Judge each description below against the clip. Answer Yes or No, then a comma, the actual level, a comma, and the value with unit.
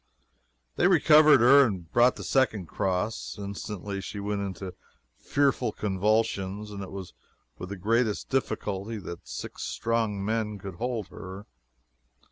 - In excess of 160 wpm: No, slow, 135 wpm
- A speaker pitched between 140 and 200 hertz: No, low, 105 Hz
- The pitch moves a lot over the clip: No, average, 3.1 semitones